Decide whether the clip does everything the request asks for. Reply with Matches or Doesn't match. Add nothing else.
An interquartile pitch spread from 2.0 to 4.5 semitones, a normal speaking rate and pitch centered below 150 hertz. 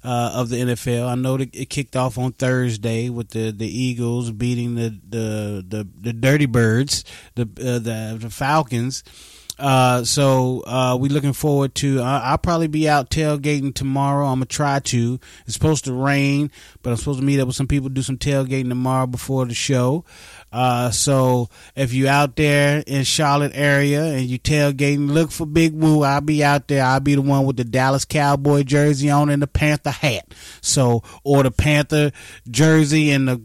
Matches